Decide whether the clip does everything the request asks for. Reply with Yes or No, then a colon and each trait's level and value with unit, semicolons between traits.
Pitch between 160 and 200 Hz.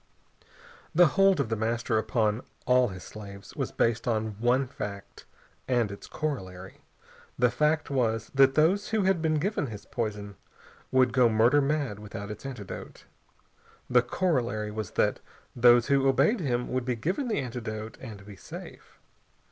No: low, 120 Hz